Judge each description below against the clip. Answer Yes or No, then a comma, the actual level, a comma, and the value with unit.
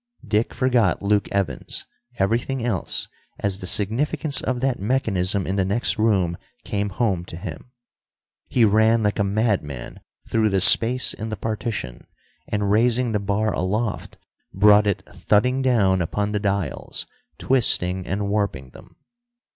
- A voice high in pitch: No, low, 105 Hz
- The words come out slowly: No, average, 145 wpm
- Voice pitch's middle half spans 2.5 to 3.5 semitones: Yes, average, 2.9 semitones